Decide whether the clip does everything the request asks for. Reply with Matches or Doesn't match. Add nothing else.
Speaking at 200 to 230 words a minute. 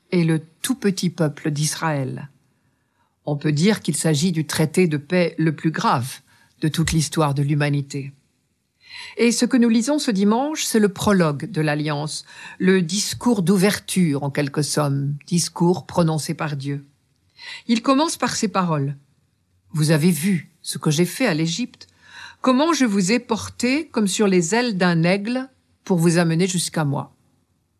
Doesn't match